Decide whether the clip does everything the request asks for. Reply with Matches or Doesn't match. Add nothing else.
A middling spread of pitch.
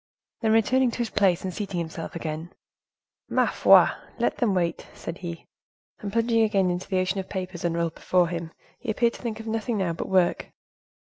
Matches